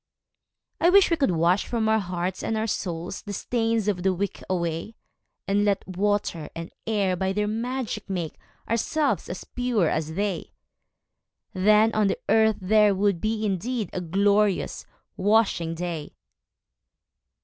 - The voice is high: Yes, high, 205 Hz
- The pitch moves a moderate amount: Yes, average, 3.3 semitones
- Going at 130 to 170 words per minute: Yes, average, 150 wpm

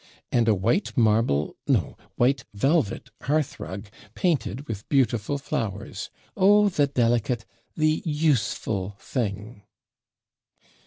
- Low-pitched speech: Yes, low, 120 Hz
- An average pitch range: No, wide, 5.7 semitones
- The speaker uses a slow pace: Yes, slow, 100 wpm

